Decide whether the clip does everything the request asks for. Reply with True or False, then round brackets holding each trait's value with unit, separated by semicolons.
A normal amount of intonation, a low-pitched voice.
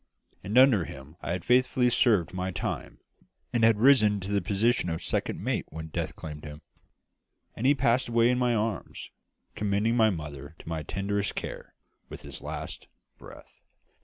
False (6.1 semitones; 105 Hz)